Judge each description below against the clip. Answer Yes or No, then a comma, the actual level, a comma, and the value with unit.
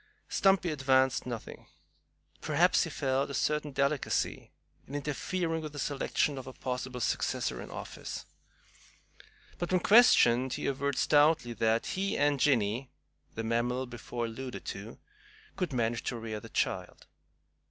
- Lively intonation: No, average, 3.6 semitones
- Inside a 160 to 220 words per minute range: No, average, 140 wpm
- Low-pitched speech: Yes, low, 130 Hz